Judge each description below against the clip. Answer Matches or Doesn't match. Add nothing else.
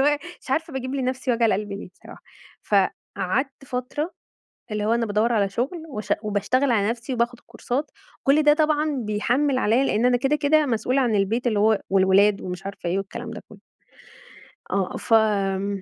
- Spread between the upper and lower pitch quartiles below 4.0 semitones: Doesn't match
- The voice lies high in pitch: Matches